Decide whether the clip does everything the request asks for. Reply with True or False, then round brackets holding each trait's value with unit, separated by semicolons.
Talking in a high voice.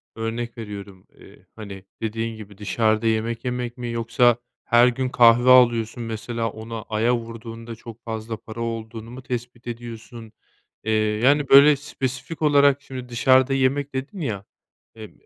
False (115 Hz)